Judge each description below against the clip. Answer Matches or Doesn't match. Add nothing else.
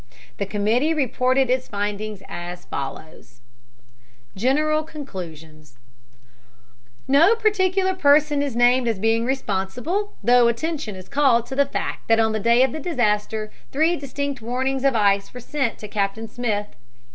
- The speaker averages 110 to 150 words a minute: Matches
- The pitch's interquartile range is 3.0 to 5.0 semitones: Doesn't match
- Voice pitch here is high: Matches